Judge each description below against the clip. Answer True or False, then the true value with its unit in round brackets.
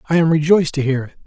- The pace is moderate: False (285 wpm)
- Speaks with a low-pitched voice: False (155 Hz)